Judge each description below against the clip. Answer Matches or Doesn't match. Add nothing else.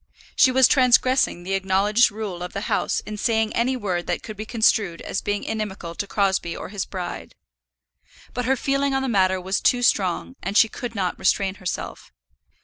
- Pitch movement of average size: Matches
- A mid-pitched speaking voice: Doesn't match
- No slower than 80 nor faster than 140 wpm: Doesn't match